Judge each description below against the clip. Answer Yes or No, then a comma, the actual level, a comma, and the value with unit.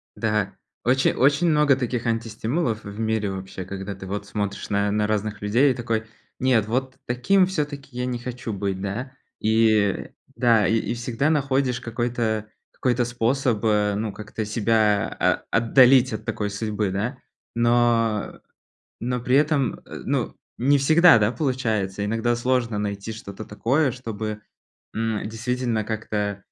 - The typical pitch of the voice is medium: No, low, 115 Hz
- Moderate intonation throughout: Yes, average, 3.2 semitones